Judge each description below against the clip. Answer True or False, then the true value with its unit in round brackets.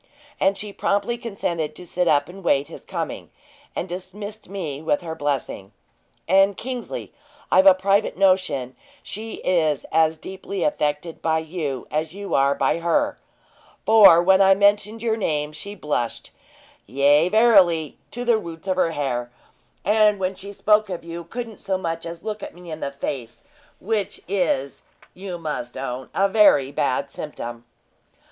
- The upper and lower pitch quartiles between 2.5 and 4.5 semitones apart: False (4.9 semitones)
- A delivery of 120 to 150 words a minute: False (160 wpm)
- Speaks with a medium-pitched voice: True (175 Hz)